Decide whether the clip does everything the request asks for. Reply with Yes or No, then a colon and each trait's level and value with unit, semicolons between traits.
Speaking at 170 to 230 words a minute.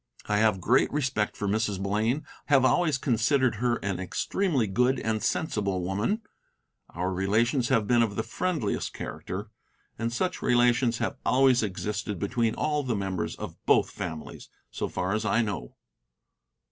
No: average, 155 wpm